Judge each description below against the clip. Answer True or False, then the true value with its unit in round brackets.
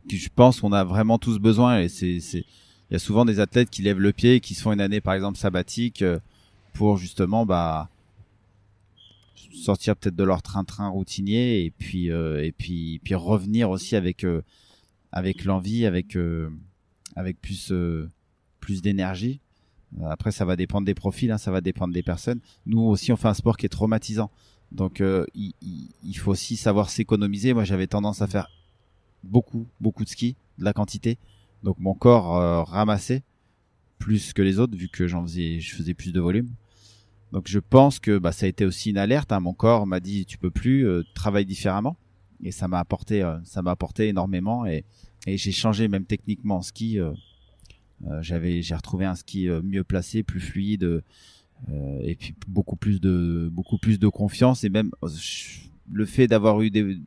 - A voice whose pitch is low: True (100 Hz)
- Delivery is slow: False (195 wpm)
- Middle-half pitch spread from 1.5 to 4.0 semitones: True (2.9 semitones)